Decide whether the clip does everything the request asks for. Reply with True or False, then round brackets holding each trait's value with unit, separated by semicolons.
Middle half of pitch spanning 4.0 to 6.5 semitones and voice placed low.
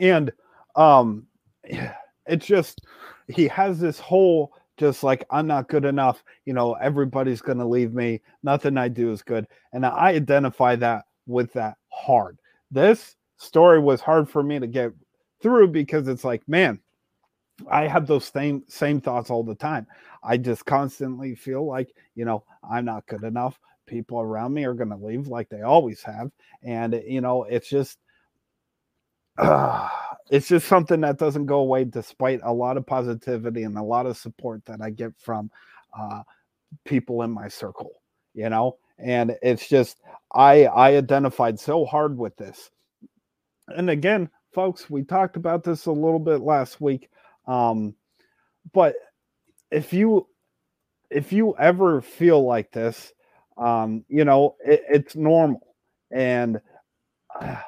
True (4.4 semitones; 130 Hz)